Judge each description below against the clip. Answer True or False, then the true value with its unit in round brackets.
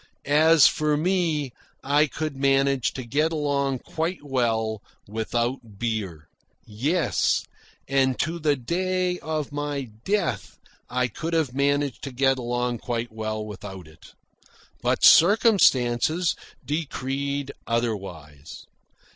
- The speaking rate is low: True (115 wpm)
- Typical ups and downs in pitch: True (4.6 semitones)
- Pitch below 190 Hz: True (135 Hz)